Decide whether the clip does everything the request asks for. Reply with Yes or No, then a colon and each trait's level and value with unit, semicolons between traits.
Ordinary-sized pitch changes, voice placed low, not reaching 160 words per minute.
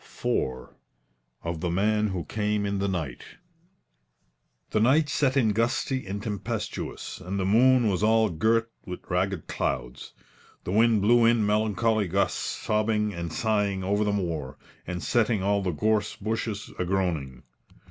Yes: average, 3.4 semitones; low, 105 Hz; average, 145 wpm